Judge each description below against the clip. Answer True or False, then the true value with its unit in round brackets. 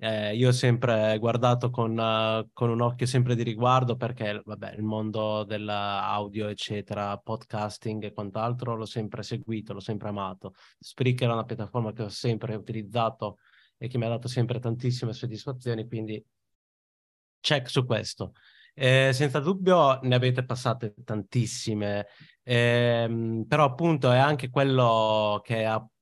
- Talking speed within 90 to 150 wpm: True (145 wpm)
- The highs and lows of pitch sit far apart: False (2.4 semitones)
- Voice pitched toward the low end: True (115 Hz)